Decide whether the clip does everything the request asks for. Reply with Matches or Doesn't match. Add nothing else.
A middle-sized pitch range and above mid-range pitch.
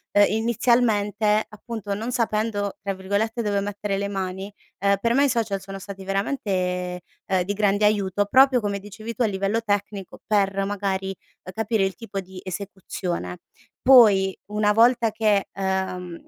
Doesn't match